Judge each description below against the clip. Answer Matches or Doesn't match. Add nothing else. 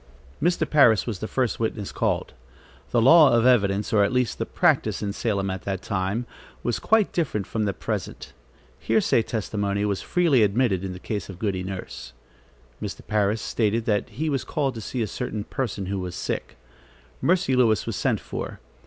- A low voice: Matches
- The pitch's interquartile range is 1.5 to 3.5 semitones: Doesn't match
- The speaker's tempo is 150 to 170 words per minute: Doesn't match